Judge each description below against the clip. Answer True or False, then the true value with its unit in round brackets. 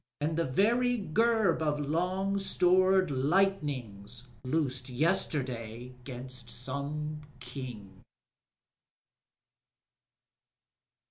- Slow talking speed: True (70 wpm)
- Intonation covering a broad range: True (6.6 semitones)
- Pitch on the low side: False (145 Hz)